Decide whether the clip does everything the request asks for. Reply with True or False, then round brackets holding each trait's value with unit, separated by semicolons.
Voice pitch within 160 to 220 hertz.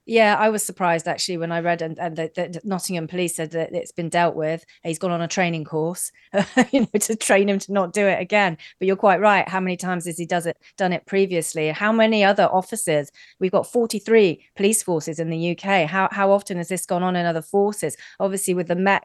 True (185 Hz)